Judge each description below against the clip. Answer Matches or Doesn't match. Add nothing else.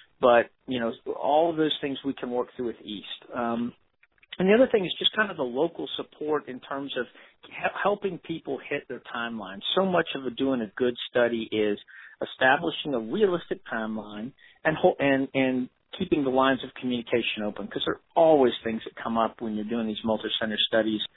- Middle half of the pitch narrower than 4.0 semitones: Doesn't match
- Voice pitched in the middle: Doesn't match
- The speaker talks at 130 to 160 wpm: Doesn't match